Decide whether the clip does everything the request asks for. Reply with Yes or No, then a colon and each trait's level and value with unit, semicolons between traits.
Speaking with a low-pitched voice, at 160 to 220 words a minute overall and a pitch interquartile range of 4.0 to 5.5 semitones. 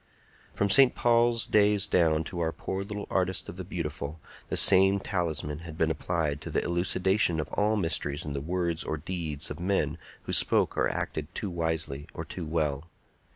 No: very low, 85 Hz; average, 185 wpm; average, 3.6 semitones